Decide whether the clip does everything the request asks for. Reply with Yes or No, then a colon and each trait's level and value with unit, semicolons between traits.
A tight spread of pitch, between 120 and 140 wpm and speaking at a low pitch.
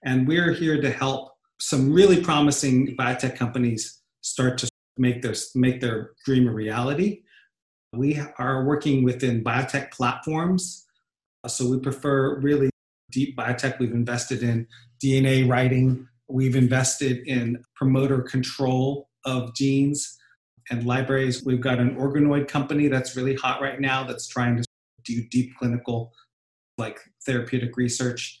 Yes: narrow, 1.8 semitones; slow, 135 wpm; low, 130 Hz